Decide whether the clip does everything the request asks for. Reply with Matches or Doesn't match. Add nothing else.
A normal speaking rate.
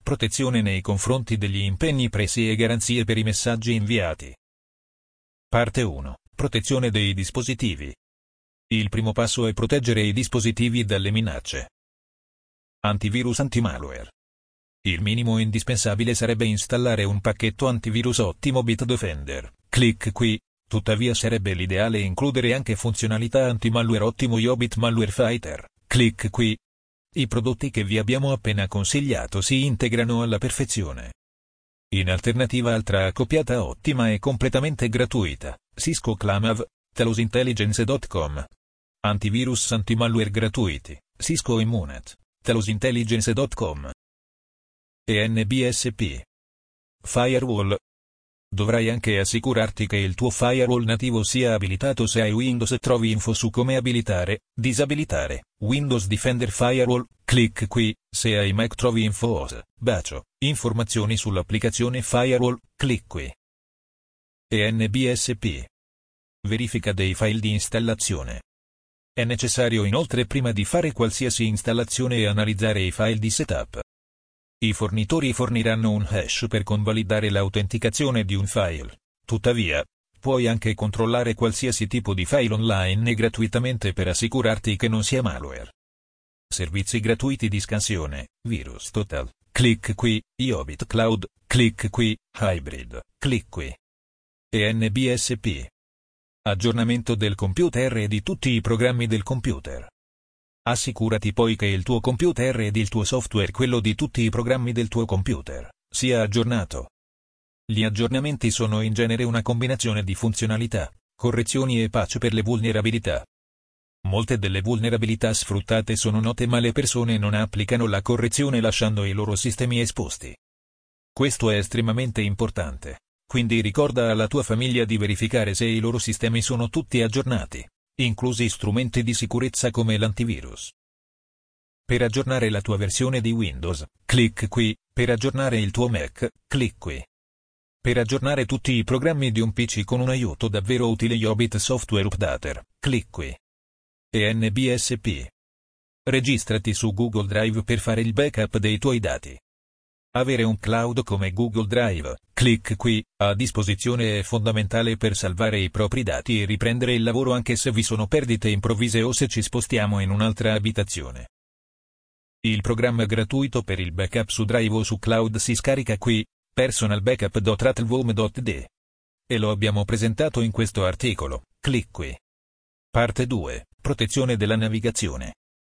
Matches